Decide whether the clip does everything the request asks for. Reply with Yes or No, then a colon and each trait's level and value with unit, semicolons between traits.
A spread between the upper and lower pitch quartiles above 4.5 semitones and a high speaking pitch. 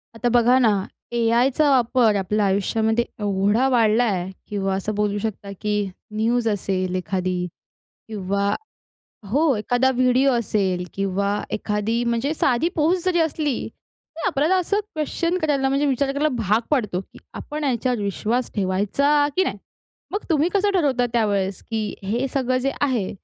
Yes: average, 5.2 semitones; high, 235 Hz